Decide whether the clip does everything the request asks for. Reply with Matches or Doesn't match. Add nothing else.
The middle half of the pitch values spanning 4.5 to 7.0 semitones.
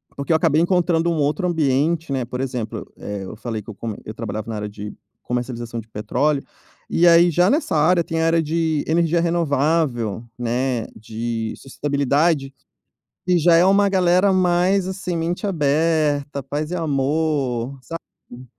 Matches